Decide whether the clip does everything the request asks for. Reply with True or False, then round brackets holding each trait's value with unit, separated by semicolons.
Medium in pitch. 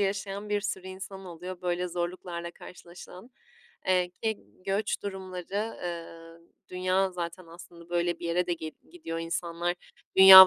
True (180 Hz)